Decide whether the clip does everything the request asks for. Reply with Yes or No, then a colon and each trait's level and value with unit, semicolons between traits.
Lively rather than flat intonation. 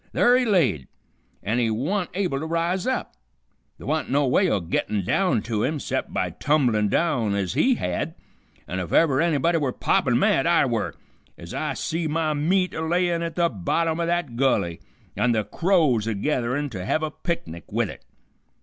Yes: wide, 7.0 semitones